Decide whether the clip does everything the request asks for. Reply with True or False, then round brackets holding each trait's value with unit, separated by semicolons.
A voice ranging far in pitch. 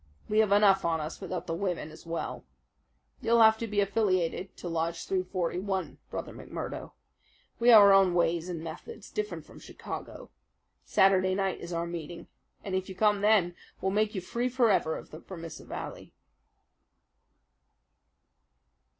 False (3.3 semitones)